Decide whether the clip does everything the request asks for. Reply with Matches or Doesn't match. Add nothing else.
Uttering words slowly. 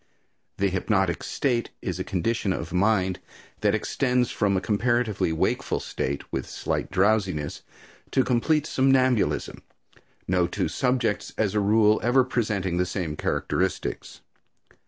Matches